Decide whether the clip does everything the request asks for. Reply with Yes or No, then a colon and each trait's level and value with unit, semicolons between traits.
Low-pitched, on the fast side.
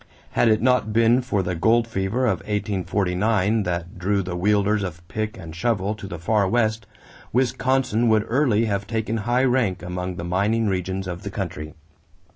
No: low, 105 Hz; average, 175 wpm